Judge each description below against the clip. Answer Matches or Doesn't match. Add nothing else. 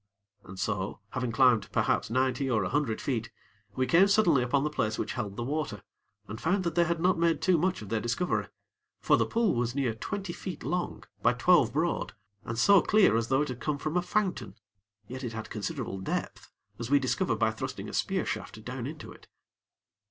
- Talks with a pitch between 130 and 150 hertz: Matches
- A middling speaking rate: Doesn't match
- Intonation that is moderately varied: Doesn't match